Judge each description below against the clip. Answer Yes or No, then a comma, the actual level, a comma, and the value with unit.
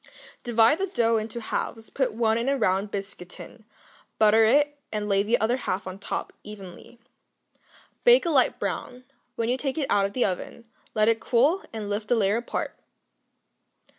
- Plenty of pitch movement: No, average, 3.4 semitones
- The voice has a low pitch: No, high, 225 Hz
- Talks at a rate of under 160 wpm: No, average, 185 wpm